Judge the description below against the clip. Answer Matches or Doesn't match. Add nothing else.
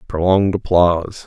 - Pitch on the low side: Matches